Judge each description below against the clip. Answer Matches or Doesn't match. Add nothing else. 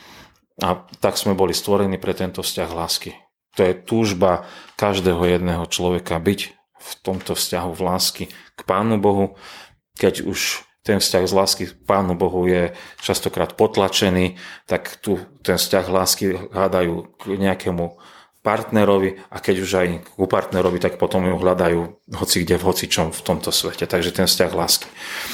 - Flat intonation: Matches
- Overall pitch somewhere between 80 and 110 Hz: Matches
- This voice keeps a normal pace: Matches